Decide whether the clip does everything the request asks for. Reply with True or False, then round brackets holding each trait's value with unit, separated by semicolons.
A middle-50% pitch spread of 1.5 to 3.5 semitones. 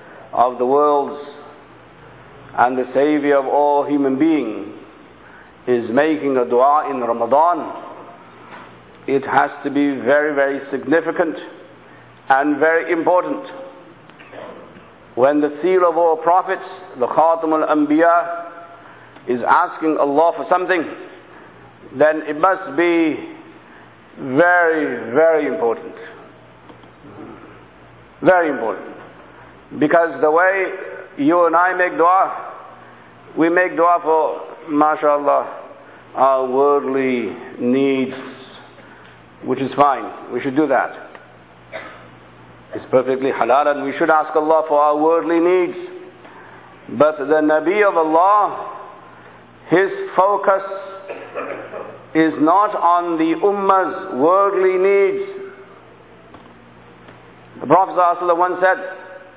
False (4.6 semitones)